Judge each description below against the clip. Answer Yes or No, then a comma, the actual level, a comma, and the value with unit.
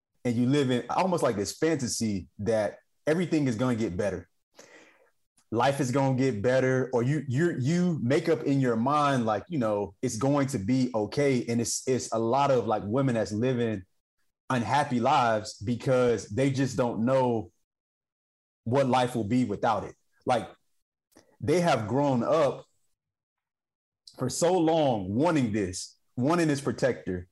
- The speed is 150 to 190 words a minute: Yes, average, 165 wpm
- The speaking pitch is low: Yes, low, 125 Hz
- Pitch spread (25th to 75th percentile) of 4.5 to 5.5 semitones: No, average, 3.7 semitones